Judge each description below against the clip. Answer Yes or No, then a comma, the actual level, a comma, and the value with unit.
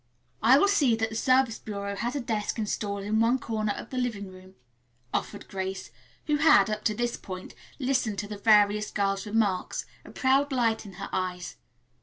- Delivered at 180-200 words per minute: Yes, average, 190 wpm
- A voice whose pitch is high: Yes, high, 215 Hz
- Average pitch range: Yes, average, 3.3 semitones